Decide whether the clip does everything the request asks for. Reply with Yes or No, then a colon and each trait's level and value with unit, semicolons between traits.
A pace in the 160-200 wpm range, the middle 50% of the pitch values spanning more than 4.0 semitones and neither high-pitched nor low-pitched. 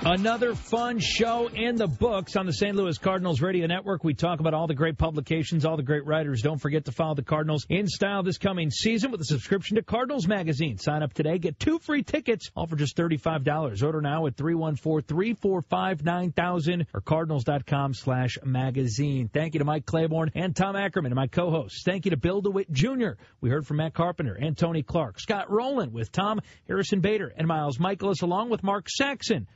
Yes: average, 195 wpm; average, 4.6 semitones; medium, 165 Hz